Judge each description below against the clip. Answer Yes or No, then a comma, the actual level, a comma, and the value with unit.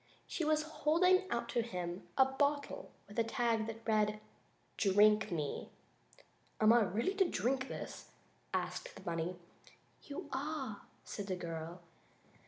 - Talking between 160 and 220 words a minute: No, average, 145 wpm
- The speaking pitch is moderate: No, high, 230 Hz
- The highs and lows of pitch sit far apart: Yes, wide, 6.3 semitones